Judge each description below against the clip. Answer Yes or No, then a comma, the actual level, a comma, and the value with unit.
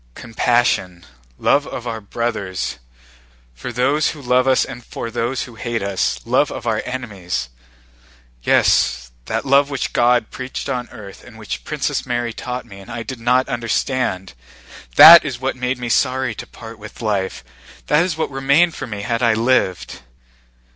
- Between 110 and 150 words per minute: No, average, 165 wpm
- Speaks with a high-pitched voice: No, low, 120 Hz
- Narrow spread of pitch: No, average, 3.4 semitones